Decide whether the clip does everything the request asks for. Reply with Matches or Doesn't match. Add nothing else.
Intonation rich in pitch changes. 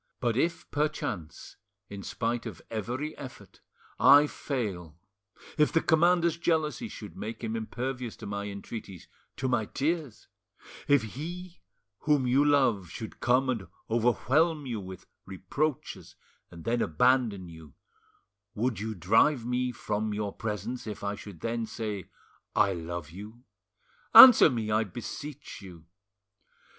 Matches